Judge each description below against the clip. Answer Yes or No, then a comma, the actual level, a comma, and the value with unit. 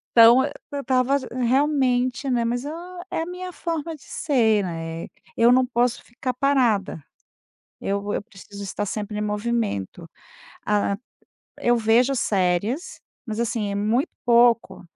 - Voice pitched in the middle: No, high, 235 Hz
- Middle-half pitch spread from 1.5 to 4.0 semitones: No, average, 4.4 semitones